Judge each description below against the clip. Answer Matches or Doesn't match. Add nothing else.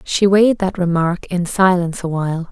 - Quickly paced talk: Doesn't match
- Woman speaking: Matches